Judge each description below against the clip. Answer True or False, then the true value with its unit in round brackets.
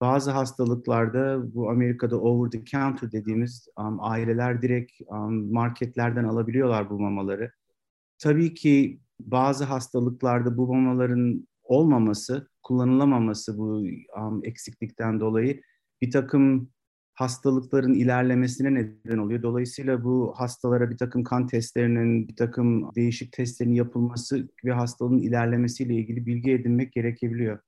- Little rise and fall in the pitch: True (1.7 semitones)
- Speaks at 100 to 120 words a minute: True (110 wpm)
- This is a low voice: True (120 Hz)